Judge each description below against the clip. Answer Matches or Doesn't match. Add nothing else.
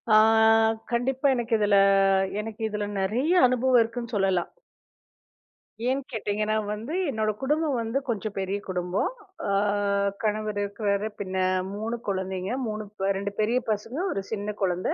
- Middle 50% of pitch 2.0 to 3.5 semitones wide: Matches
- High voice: Matches